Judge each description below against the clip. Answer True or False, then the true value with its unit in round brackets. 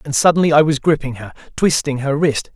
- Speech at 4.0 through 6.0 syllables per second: True (5.9 syllables/s)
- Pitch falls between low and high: True (145 Hz)